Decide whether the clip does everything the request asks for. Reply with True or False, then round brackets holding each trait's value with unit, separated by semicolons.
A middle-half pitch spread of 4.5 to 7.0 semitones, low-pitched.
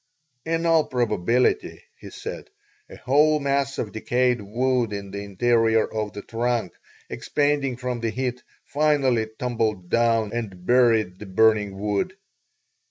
False (3.6 semitones; 120 Hz)